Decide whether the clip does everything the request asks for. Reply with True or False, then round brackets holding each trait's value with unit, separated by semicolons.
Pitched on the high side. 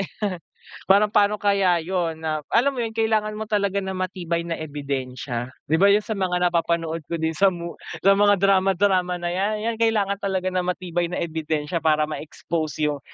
False (180 Hz)